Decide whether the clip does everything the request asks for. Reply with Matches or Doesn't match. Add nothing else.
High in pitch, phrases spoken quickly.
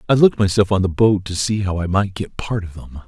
Doesn't match